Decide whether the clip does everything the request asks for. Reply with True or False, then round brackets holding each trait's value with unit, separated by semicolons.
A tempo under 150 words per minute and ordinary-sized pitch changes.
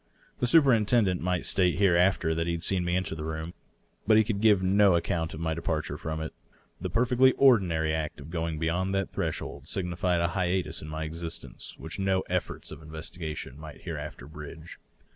False (195 wpm; 3.2 semitones)